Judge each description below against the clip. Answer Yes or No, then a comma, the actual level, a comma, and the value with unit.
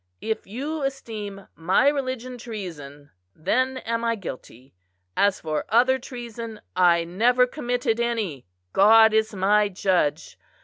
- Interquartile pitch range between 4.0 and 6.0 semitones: Yes, average, 4.7 semitones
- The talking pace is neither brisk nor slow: No, slow, 125 wpm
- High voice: Yes, high, 220 Hz